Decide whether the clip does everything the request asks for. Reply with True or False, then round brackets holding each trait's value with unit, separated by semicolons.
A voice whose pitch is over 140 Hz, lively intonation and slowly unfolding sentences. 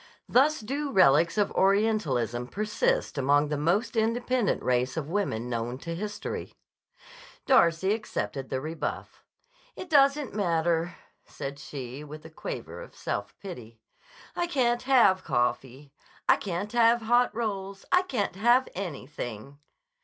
True (185 Hz; 8.6 semitones; 130 wpm)